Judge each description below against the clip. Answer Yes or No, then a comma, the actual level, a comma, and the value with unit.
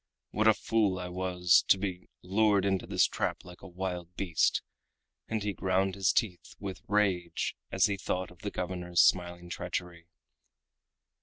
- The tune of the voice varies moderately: No, narrow, 1.9 semitones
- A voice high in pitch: No, very low, 95 Hz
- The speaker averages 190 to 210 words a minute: No, average, 160 wpm